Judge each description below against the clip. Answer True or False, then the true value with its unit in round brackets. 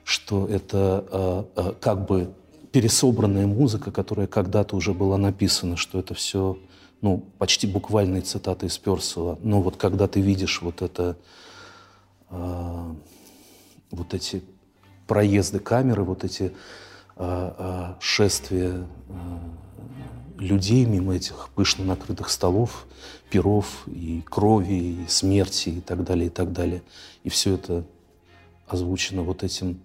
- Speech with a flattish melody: True (1.8 semitones)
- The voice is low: True (95 Hz)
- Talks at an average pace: True (125 wpm)